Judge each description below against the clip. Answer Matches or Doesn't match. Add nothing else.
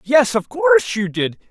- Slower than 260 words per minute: Matches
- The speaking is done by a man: Matches